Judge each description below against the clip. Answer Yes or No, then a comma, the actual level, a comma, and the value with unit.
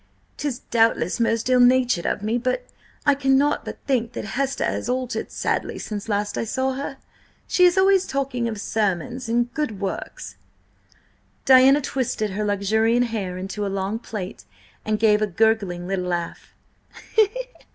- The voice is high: Yes, high, 230 Hz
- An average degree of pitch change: Yes, average, 4.1 semitones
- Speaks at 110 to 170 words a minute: Yes, average, 155 wpm